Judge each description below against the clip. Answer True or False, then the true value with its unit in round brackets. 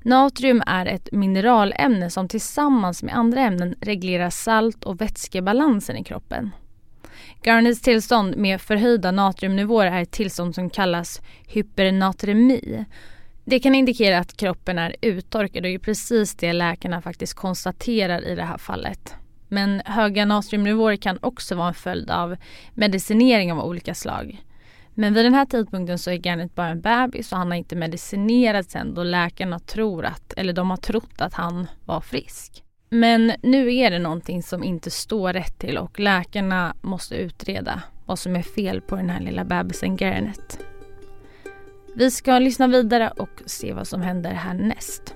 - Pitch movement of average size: True (4.7 semitones)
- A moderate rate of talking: True (160 wpm)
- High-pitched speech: True (195 Hz)